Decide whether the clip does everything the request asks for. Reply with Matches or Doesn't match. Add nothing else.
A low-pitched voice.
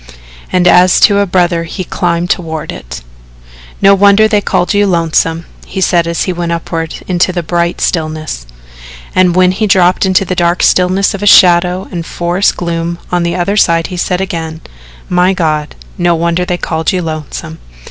Doesn't match